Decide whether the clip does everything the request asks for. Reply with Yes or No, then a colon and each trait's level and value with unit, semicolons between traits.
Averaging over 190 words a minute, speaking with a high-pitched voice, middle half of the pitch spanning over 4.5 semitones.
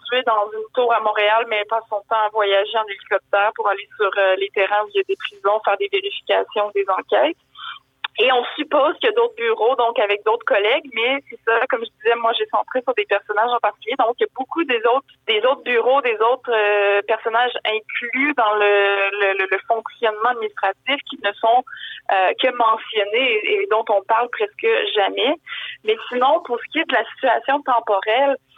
Yes: average, 200 wpm; high, 230 Hz; average, 4.9 semitones